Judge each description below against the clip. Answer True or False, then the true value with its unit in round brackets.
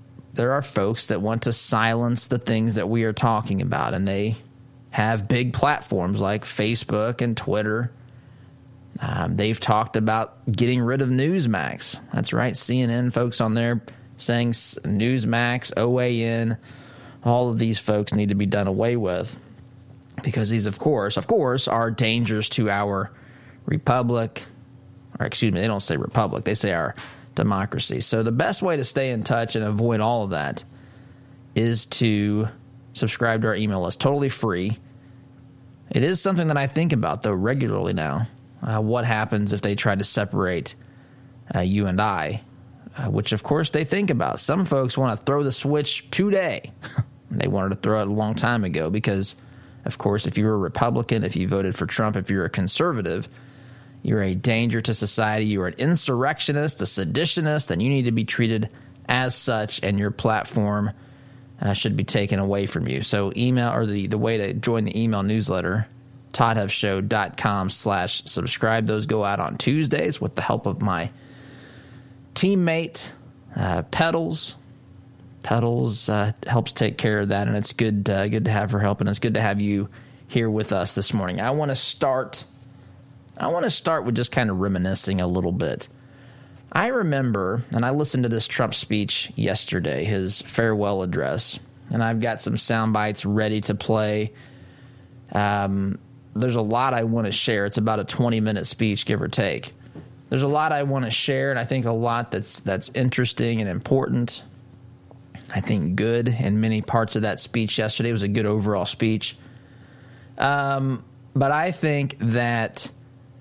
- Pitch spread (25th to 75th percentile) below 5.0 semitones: True (3.6 semitones)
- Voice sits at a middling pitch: False (115 Hz)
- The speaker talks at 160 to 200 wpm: True (175 wpm)